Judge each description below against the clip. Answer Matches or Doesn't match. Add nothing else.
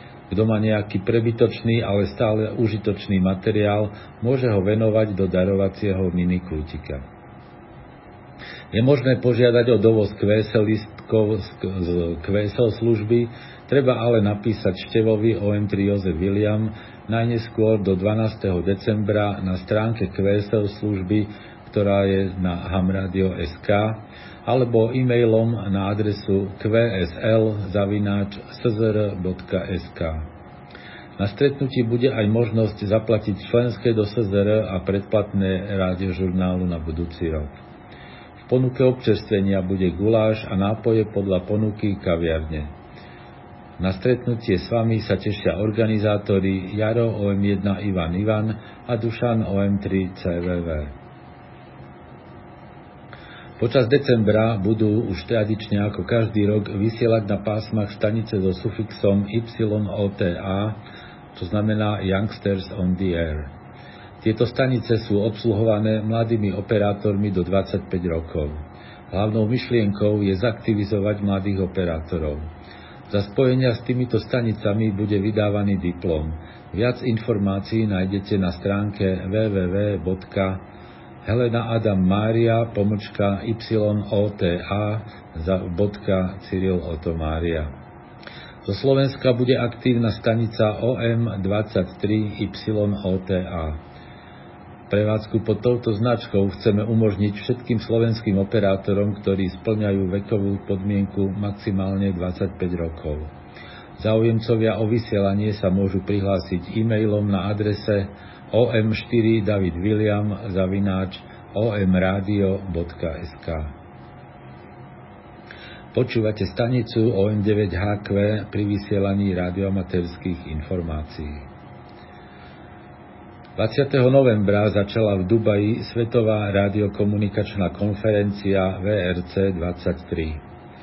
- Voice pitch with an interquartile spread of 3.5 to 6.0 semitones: Doesn't match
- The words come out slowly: Matches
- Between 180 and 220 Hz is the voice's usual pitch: Doesn't match